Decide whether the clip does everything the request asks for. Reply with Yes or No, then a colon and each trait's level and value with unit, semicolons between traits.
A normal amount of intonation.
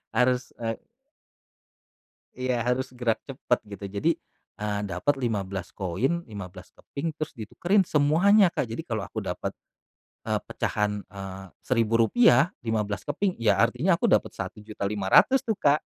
No: wide, 6.0 semitones